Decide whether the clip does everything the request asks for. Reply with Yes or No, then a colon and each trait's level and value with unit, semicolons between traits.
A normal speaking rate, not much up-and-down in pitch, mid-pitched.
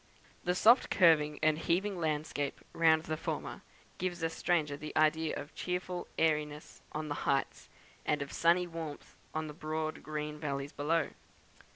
Yes: average, 155 wpm; narrow, 1.9 semitones; medium, 155 Hz